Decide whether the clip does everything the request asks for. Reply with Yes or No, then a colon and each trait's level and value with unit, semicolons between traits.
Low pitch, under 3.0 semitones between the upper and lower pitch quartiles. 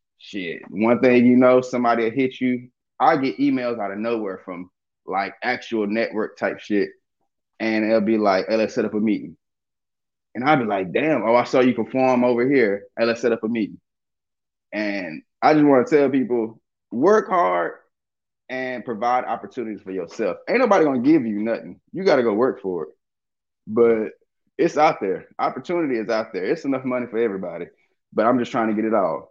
Yes: low, 115 Hz; narrow, 2.5 semitones